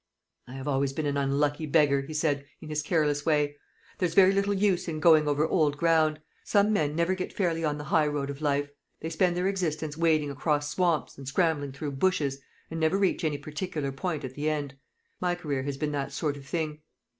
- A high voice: No, medium, 150 Hz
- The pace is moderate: No, fast, 215 wpm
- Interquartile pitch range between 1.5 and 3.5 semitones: Yes, average, 2.7 semitones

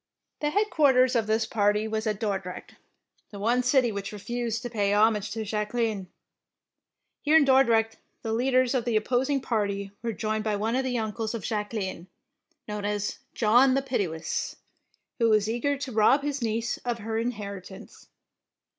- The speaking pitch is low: No, high, 225 Hz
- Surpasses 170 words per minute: No, average, 165 wpm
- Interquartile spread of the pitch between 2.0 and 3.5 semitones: Yes, average, 3.0 semitones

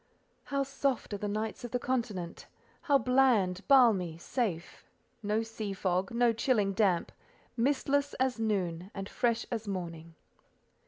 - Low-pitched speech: No, high, 220 Hz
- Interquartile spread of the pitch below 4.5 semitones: No, average, 4.9 semitones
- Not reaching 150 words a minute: Yes, average, 140 wpm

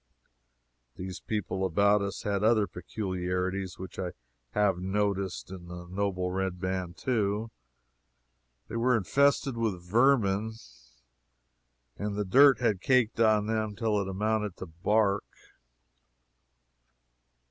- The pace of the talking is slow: Yes, slow, 115 wpm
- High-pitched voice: No, low, 100 Hz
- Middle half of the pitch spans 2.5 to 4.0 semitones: Yes, average, 2.9 semitones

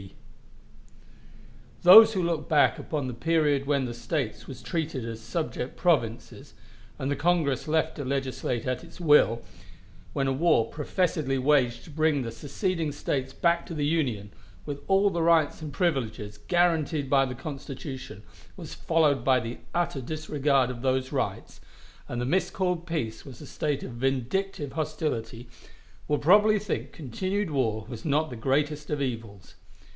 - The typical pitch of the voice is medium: Yes, medium, 145 Hz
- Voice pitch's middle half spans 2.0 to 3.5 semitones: No, average, 4.3 semitones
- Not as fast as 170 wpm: Yes, average, 155 wpm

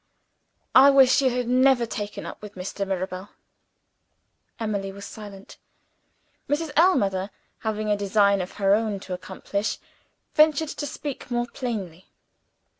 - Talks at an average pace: No, slow, 130 wpm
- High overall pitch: Yes, high, 210 Hz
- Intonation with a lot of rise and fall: No, average, 4.7 semitones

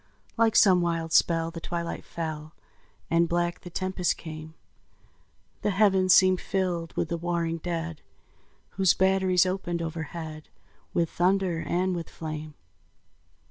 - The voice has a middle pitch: Yes, medium, 170 Hz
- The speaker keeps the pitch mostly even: Yes, narrow, 2.2 semitones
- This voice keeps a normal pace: No, slow, 130 wpm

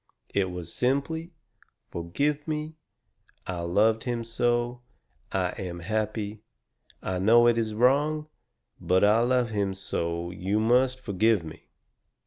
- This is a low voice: Yes, low, 110 Hz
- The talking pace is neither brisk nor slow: No, slow, 125 wpm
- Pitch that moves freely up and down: No, average, 5.0 semitones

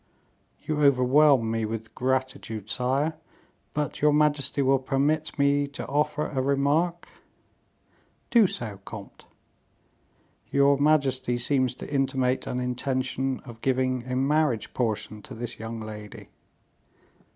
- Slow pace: Yes, slow, 120 wpm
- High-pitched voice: No, low, 130 Hz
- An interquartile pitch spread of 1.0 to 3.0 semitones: Yes, average, 2.7 semitones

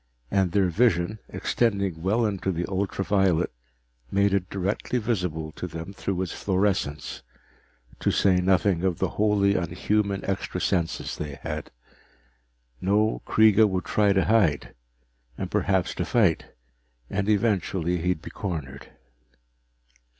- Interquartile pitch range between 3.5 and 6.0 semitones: No, narrow, 2.6 semitones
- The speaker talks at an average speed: No, slow, 130 wpm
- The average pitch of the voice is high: No, very low, 95 Hz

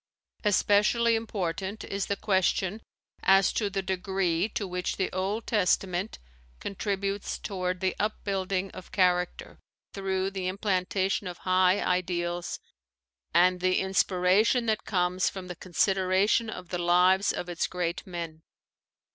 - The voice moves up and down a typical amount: No, narrow, 1.7 semitones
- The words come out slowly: Yes, slow, 130 wpm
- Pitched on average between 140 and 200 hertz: Yes, high, 190 Hz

